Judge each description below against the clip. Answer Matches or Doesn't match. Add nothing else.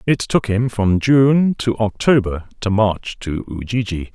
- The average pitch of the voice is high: Doesn't match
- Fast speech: Doesn't match